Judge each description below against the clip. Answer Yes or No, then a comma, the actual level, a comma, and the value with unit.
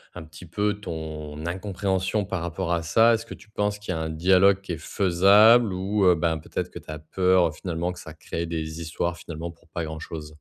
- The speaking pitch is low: Yes, very low, 85 Hz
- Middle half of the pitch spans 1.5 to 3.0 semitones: No, average, 3.4 semitones